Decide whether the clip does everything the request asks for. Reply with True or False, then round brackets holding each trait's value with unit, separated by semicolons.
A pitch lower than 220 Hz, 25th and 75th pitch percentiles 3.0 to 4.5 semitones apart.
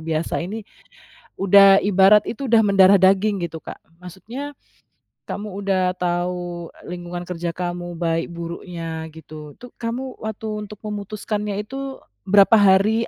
True (190 Hz; 3.3 semitones)